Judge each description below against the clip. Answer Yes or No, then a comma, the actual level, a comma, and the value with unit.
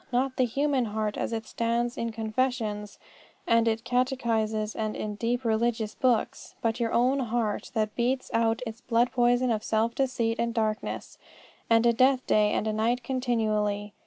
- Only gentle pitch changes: Yes, narrow, 2.1 semitones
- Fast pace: No, average, 160 wpm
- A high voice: Yes, high, 230 Hz